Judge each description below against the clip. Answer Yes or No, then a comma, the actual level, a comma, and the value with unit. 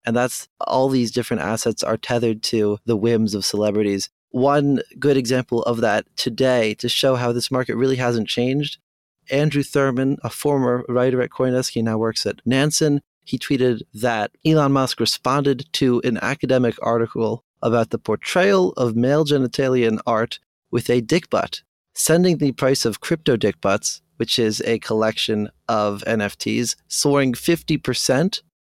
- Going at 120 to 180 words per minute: Yes, average, 155 wpm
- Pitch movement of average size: Yes, average, 3.2 semitones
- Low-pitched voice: Yes, low, 125 Hz